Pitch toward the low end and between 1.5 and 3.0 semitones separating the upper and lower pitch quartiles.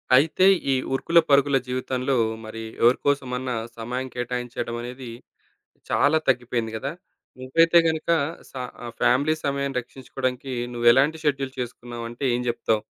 Yes: low, 130 Hz; narrow, 2.4 semitones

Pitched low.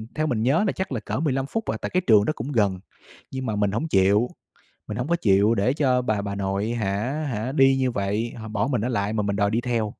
Yes: low, 115 Hz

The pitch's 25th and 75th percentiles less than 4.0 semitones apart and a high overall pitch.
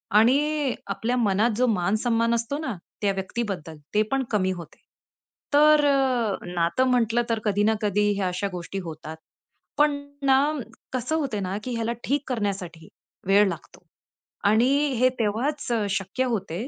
No: average, 4.7 semitones; high, 220 Hz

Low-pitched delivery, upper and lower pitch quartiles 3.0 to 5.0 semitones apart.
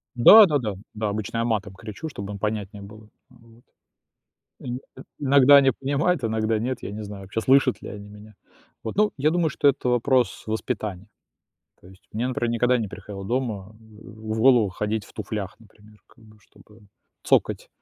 Yes: low, 110 Hz; average, 3.4 semitones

